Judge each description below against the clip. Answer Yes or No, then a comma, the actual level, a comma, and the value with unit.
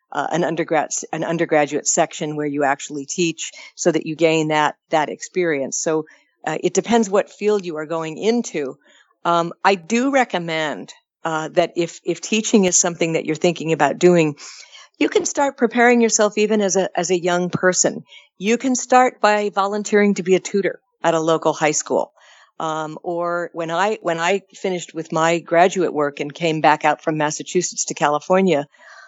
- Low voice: No, medium, 175 Hz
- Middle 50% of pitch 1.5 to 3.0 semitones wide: No, average, 4.2 semitones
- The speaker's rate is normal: Yes, average, 180 wpm